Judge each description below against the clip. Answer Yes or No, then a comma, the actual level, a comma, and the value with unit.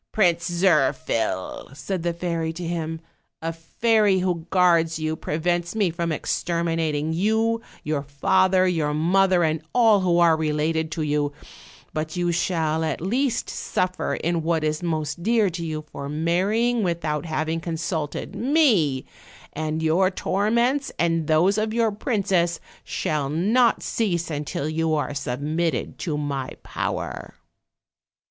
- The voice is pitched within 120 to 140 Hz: No, medium, 165 Hz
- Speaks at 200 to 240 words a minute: No, average, 140 wpm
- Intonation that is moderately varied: Yes, average, 3.2 semitones